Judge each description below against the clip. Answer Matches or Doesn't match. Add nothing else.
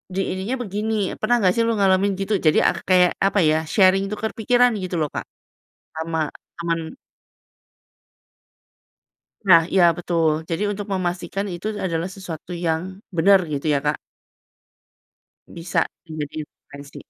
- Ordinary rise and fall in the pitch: Matches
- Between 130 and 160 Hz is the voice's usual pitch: Doesn't match